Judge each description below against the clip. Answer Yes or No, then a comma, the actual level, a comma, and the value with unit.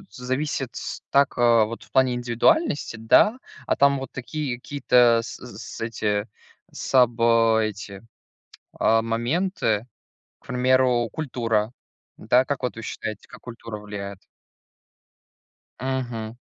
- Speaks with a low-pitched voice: Yes, low, 120 Hz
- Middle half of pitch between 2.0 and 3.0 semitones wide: Yes, narrow, 2.6 semitones